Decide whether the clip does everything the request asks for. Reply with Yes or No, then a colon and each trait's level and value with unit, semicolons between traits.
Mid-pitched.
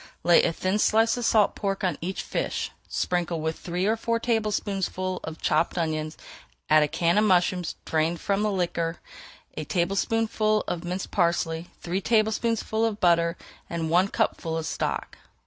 Yes: medium, 180 Hz